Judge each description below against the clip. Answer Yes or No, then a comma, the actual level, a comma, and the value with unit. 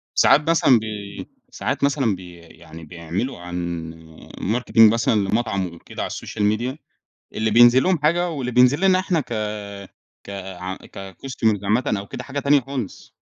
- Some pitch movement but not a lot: No, wide, 5.8 semitones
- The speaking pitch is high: No, low, 110 Hz